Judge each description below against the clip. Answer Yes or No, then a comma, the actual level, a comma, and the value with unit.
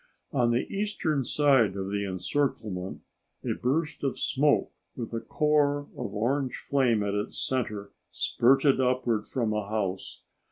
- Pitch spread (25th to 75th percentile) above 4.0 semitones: Yes, average, 5.1 semitones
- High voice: No, low, 125 Hz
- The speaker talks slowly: No, average, 145 wpm